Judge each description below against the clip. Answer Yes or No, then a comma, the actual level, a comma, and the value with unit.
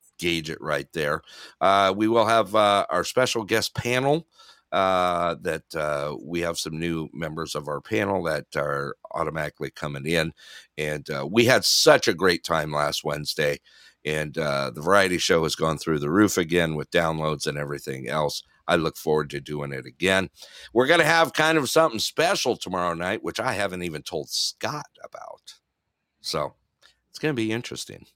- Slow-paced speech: No, average, 180 wpm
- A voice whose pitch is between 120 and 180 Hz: No, very low, 85 Hz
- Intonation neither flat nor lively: No, wide, 6.6 semitones